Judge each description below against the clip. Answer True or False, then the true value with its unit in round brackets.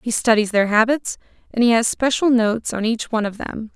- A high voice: True (230 Hz)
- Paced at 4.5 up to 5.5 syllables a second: False (5.7 syllables/s)